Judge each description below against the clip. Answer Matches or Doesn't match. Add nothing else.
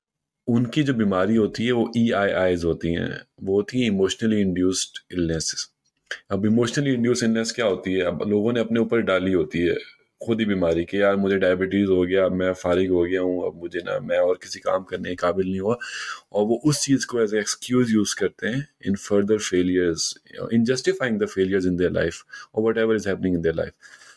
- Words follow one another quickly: Matches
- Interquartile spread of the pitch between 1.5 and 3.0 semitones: Doesn't match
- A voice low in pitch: Matches